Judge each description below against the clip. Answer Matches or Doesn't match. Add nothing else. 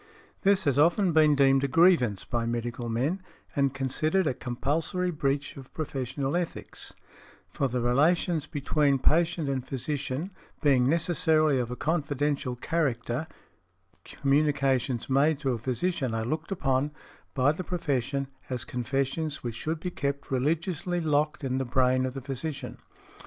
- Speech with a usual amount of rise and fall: Matches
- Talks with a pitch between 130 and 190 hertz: Matches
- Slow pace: Doesn't match